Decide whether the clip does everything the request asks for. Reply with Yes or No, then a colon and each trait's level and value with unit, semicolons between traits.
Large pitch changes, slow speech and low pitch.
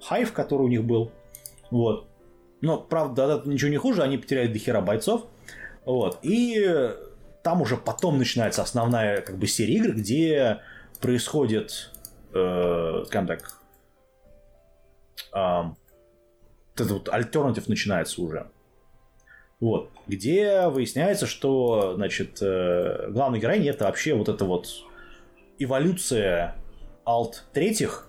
Yes: wide, 6.5 semitones; slow, 105 wpm; low, 120 Hz